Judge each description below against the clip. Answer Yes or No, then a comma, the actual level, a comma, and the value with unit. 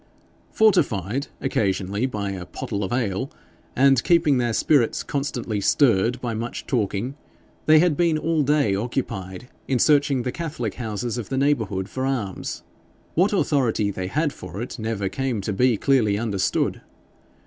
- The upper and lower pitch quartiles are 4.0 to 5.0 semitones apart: No, wide, 5.5 semitones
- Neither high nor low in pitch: No, low, 120 Hz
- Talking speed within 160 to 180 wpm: No, average, 150 wpm